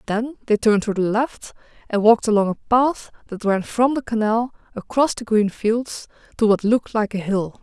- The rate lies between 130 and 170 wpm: No, fast, 205 wpm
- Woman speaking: Yes, female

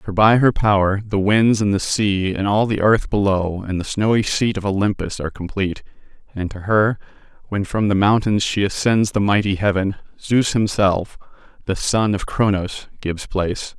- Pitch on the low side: Yes, low, 100 Hz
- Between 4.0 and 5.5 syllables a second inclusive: Yes, 4.9 syllables/s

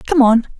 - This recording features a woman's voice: Yes, female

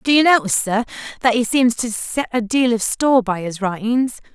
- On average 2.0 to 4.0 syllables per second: No, 5.4 syllables/s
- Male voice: No, female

